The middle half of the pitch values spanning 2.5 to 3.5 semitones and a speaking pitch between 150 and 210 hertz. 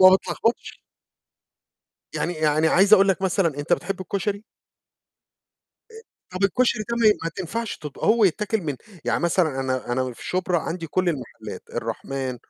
No: average, 4.8 semitones; medium, 185 Hz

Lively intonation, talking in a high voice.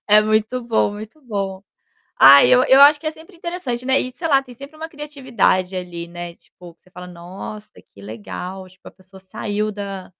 Yes: wide, 6.4 semitones; high, 205 Hz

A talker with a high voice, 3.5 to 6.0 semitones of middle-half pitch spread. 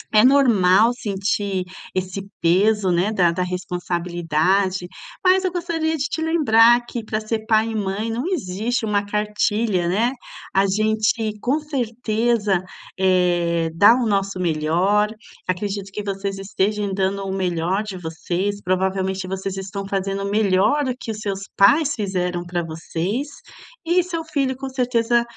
Yes: high, 200 Hz; average, 3.8 semitones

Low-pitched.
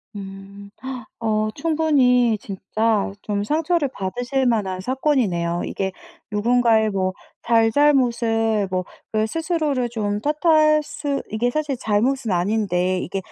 No: high, 225 Hz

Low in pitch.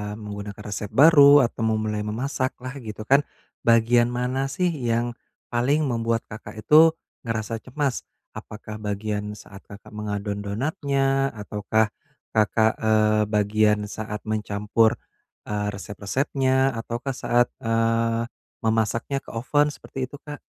Yes: low, 115 Hz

